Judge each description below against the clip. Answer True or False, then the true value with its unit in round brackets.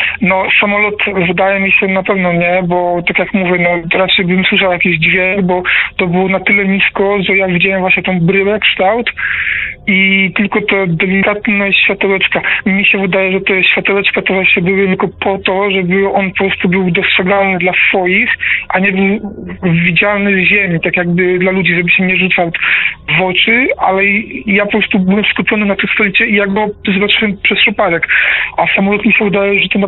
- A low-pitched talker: False (195 Hz)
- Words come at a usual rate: False (190 wpm)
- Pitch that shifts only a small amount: True (1.5 semitones)